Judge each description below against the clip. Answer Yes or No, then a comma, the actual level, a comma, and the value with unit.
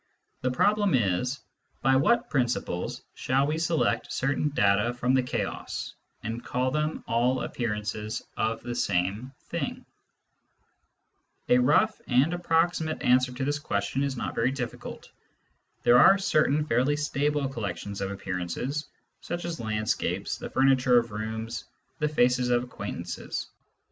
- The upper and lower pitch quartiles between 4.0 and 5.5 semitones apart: Yes, average, 4.3 semitones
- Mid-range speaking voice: No, low, 125 Hz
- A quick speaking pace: No, average, 140 wpm